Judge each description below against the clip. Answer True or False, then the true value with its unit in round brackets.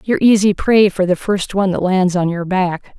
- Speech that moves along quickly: True (240 wpm)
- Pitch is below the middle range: False (190 Hz)